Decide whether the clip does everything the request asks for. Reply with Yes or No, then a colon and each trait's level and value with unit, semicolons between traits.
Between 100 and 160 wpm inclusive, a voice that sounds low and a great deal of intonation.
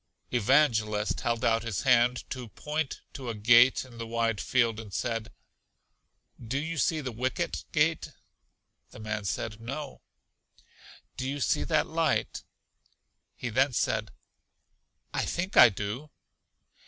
No: slow, 135 wpm; low, 120 Hz; average, 3.4 semitones